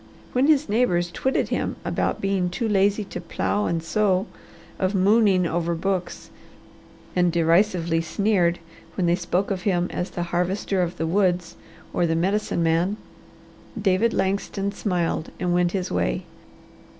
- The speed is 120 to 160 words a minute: Yes, average, 150 wpm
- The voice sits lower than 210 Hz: Yes, medium, 185 Hz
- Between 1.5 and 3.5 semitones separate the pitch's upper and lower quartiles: Yes, narrow, 2.6 semitones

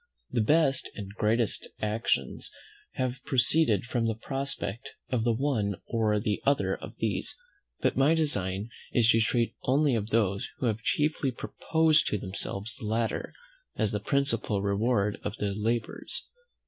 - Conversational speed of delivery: Yes, average, 150 wpm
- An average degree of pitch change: Yes, average, 4.1 semitones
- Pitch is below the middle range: Yes, low, 115 Hz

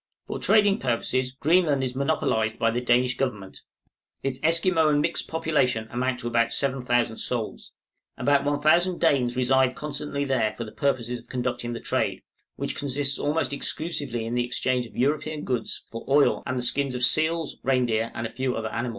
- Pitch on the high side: No, low, 130 Hz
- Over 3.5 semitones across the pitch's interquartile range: No, average, 3.2 semitones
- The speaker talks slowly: No, average, 175 wpm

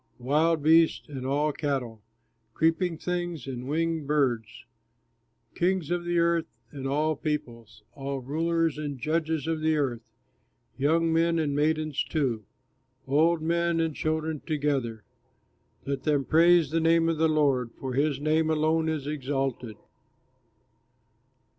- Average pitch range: Yes, average, 3.0 semitones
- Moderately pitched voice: Yes, medium, 155 Hz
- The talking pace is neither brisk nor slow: No, slow, 130 wpm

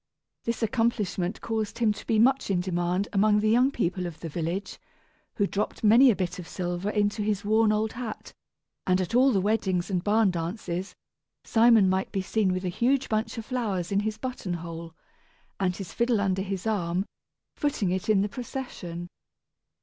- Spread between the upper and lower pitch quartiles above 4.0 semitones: No, average, 3.6 semitones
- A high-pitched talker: Yes, high, 205 Hz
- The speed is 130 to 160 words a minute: No, average, 180 wpm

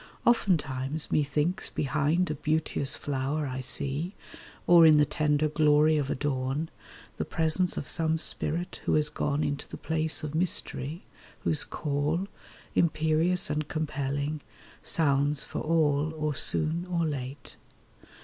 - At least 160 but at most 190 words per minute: No, slow, 135 wpm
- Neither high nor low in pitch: Yes, medium, 150 Hz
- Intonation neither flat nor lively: No, narrow, 2.1 semitones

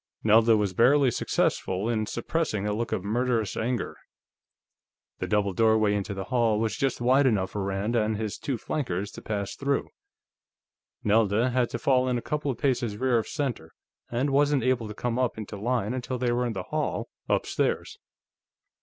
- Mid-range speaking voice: No, low, 115 Hz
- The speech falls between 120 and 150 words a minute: No, average, 180 wpm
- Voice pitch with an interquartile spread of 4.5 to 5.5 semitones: No, average, 3.4 semitones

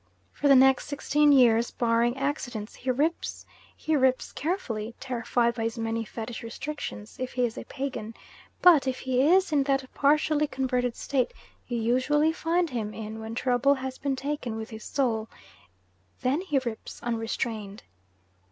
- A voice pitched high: Yes, very high, 255 Hz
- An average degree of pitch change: Yes, average, 3.7 semitones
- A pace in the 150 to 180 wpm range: Yes, average, 160 wpm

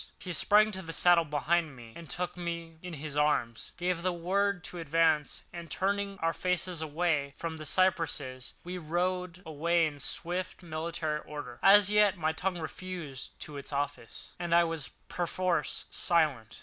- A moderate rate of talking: Yes, average, 160 wpm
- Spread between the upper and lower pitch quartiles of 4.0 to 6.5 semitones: No, average, 3.1 semitones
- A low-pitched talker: No, medium, 170 Hz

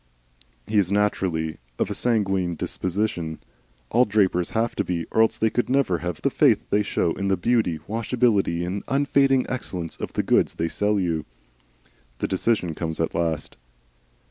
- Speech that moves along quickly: No, average, 170 wpm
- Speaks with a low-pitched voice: Yes, very low, 95 Hz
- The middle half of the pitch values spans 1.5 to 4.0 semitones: No, average, 4.7 semitones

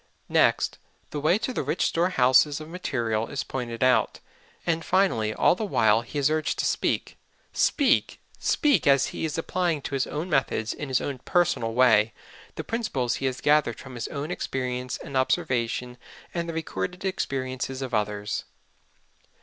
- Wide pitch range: No, average, 5.0 semitones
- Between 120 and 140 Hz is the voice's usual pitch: Yes, low, 135 Hz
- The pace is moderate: Yes, average, 165 wpm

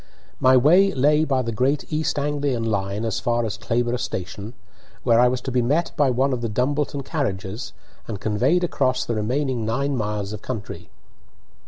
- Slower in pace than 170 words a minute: No, average, 180 wpm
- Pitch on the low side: Yes, low, 125 Hz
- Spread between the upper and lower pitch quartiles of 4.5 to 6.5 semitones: No, average, 4.1 semitones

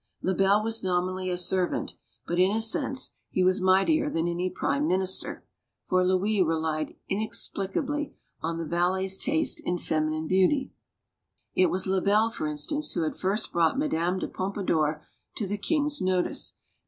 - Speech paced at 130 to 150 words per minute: No, average, 160 wpm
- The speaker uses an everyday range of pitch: Yes, average, 3.6 semitones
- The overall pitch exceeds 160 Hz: Yes, medium, 185 Hz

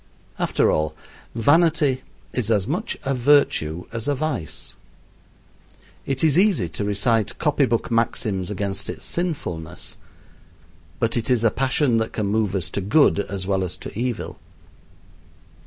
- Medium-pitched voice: No, low, 115 Hz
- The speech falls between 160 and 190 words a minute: No, average, 145 wpm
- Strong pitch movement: Yes, wide, 6.1 semitones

